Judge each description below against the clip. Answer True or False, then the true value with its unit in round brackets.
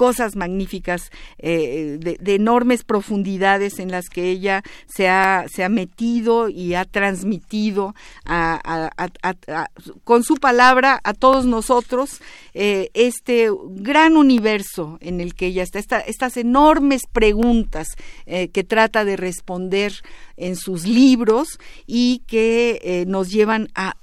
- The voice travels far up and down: False (4.5 semitones)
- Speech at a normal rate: True (140 wpm)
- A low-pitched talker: False (205 Hz)